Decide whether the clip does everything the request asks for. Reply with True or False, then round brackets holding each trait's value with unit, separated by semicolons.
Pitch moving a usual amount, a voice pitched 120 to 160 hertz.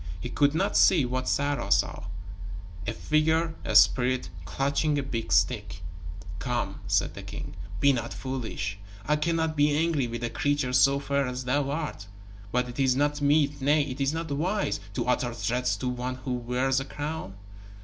True (3.0 semitones; 135 Hz)